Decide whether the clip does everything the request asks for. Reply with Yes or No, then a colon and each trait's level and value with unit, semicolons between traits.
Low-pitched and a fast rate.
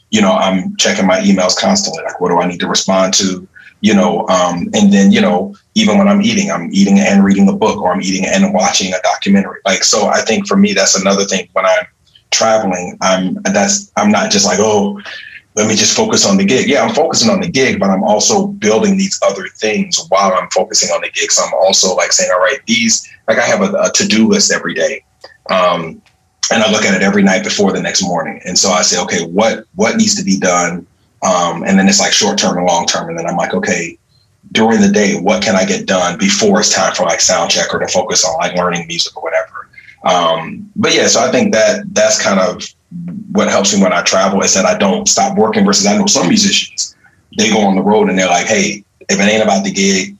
No: high, 195 Hz; fast, 245 wpm